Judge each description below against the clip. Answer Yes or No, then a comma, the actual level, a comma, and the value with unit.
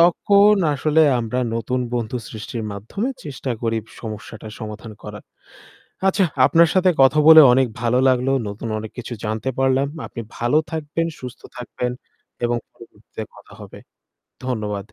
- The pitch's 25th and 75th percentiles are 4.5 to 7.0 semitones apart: Yes, average, 5.0 semitones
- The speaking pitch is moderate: No, low, 125 Hz